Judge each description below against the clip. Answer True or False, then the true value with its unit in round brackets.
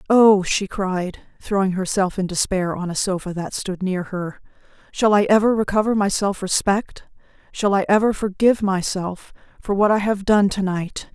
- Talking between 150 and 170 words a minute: False (180 wpm)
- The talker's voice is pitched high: True (195 Hz)